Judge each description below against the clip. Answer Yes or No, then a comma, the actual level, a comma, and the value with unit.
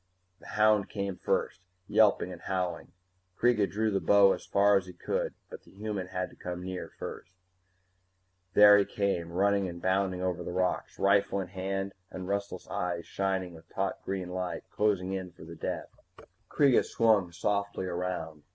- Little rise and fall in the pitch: Yes, narrow, 1.9 semitones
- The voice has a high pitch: No, very low, 95 Hz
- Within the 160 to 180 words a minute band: Yes, average, 170 wpm